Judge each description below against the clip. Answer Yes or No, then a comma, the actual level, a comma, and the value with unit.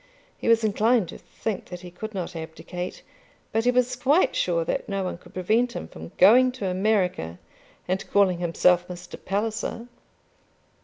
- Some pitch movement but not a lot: Yes, average, 4.0 semitones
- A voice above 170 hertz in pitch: Yes, high, 190 Hz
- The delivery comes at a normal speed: Yes, average, 165 wpm